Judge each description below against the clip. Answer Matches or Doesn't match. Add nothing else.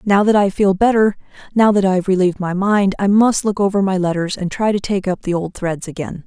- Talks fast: Matches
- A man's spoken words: Doesn't match